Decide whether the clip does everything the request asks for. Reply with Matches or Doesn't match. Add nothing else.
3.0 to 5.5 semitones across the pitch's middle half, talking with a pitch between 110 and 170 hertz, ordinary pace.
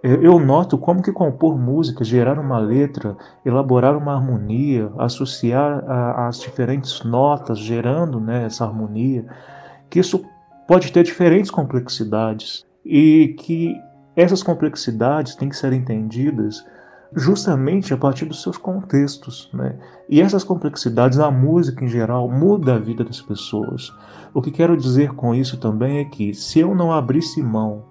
Matches